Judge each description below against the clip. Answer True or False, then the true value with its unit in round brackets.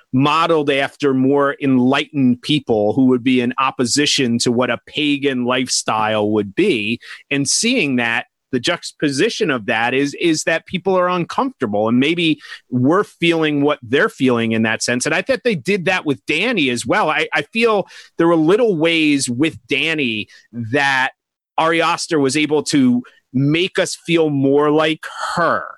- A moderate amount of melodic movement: True (4.4 semitones)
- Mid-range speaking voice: True (145 Hz)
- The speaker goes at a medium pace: True (165 wpm)